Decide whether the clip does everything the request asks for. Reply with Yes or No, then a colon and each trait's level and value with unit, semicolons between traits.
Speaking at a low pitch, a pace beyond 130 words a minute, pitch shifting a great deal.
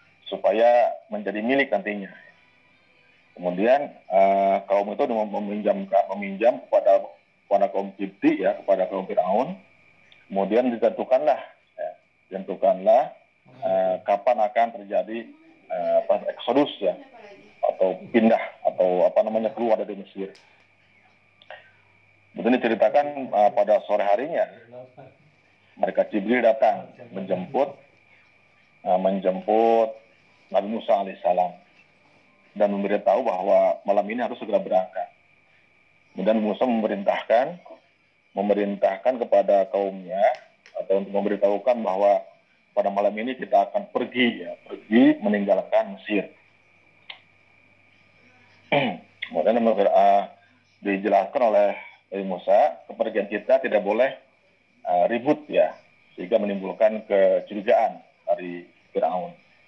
No: low, 105 Hz; average, 100 wpm; wide, 5.8 semitones